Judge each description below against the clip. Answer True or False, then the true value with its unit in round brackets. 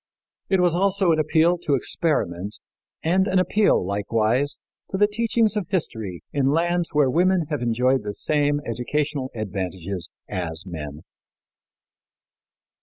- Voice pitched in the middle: True (145 Hz)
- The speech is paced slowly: True (130 wpm)